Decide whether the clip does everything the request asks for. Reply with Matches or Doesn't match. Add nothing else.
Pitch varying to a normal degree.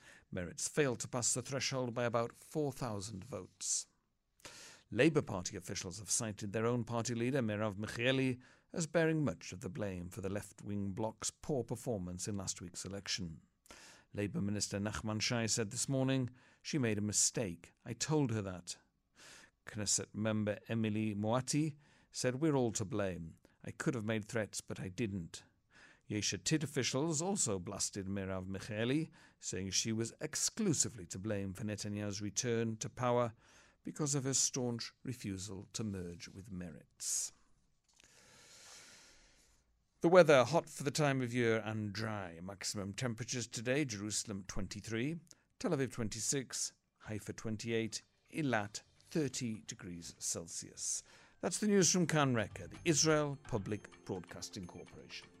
Matches